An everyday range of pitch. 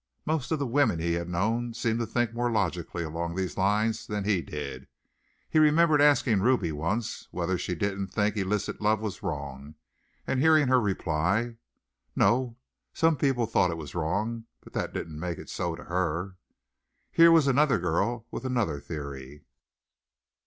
No: wide, 6.1 semitones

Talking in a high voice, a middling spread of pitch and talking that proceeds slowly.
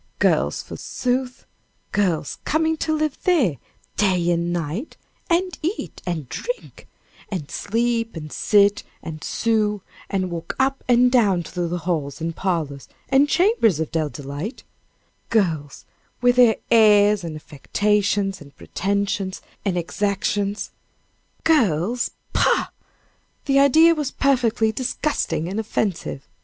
No: high, 205 Hz; wide, 6.6 semitones; slow, 125 wpm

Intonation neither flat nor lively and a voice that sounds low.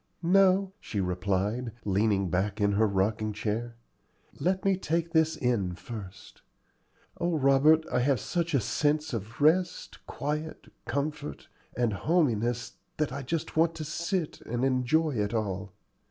No: wide, 7.2 semitones; low, 125 Hz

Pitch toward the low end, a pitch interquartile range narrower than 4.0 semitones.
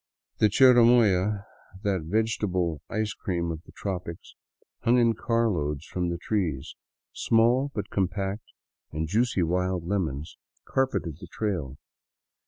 No: very low, 95 Hz; average, 4.7 semitones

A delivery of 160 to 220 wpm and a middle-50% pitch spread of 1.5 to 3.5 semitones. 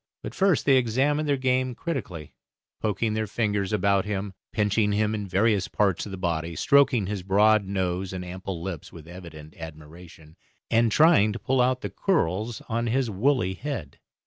No: average, 170 wpm; average, 4.7 semitones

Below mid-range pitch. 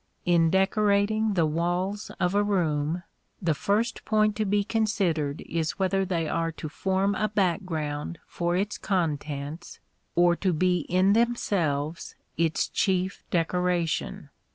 No: medium, 180 Hz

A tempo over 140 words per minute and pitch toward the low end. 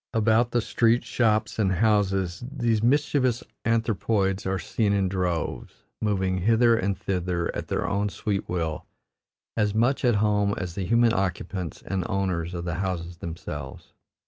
Yes: average, 150 wpm; low, 100 Hz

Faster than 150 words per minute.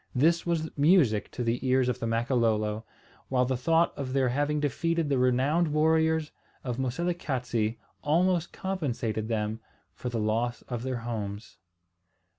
No: average, 145 wpm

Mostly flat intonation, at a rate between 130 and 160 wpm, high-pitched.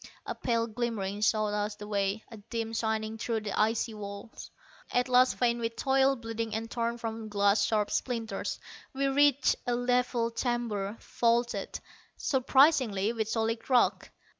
Yes: narrow, 2.3 semitones; average, 150 wpm; high, 230 Hz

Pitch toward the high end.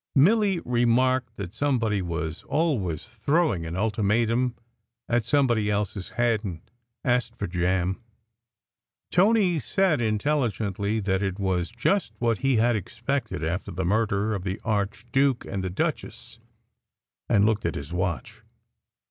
No: low, 110 Hz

